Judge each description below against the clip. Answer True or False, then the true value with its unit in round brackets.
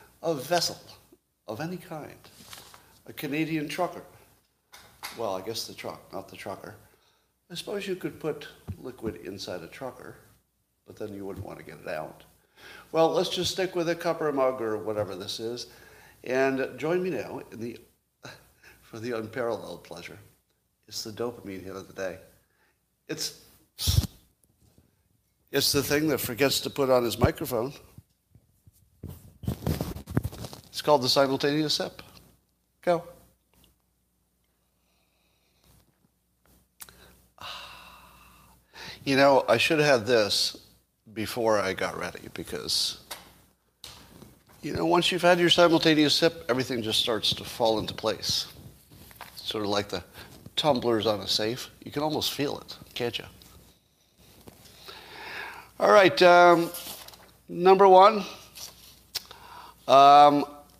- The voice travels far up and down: True (7.3 semitones)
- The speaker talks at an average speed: False (130 wpm)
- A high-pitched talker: False (135 Hz)